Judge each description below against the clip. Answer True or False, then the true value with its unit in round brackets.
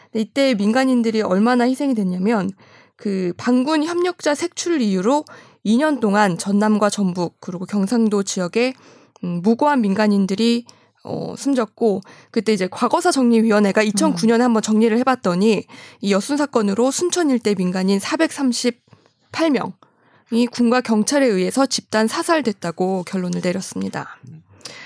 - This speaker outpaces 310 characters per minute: False (285 characters per minute)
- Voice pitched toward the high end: True (225 Hz)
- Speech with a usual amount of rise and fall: True (4.3 semitones)